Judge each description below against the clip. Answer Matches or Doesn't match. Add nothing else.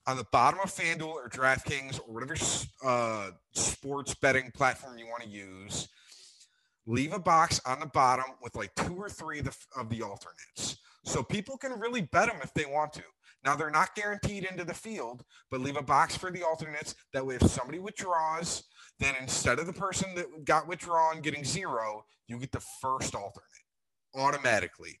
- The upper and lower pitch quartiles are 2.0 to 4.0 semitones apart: Doesn't match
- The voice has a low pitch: Doesn't match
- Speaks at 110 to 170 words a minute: Doesn't match